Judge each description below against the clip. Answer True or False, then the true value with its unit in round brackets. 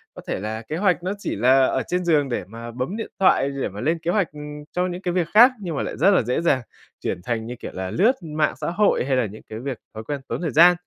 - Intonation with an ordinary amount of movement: False (6.6 semitones)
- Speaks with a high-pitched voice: False (150 Hz)